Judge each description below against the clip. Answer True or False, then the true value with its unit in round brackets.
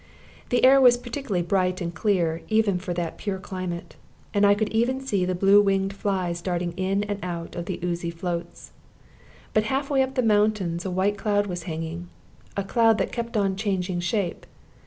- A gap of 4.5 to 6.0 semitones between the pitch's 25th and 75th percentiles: False (3.5 semitones)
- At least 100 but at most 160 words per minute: False (190 wpm)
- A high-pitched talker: True (195 Hz)